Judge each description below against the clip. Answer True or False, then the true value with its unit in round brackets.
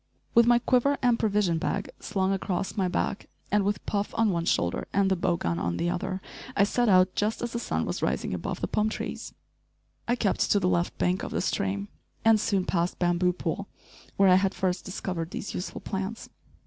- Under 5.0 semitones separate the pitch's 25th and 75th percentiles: True (2.8 semitones)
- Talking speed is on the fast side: True (210 wpm)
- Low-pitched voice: False (195 Hz)